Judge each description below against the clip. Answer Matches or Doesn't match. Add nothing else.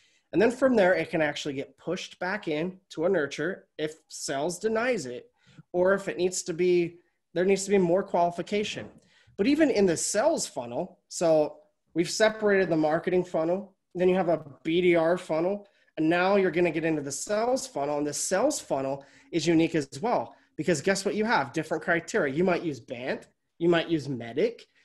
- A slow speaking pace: Doesn't match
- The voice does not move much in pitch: Doesn't match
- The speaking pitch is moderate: Matches